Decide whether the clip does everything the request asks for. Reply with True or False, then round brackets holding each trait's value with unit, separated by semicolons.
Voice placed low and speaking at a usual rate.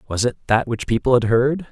False (120 Hz; 245 wpm)